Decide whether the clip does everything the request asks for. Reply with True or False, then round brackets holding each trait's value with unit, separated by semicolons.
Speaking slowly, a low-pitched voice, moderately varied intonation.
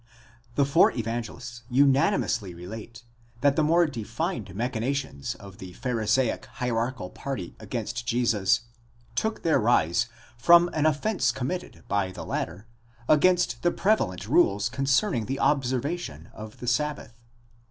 True (130 wpm; 120 Hz; 4.6 semitones)